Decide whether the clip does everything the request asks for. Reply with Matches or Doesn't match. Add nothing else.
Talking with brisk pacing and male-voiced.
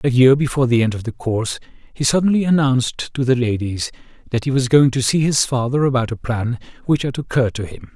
Matches